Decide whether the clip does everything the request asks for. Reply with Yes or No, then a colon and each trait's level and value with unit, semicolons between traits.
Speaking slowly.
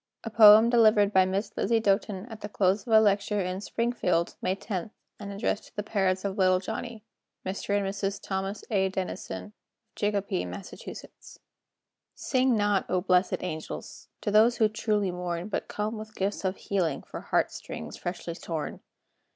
No: average, 170 wpm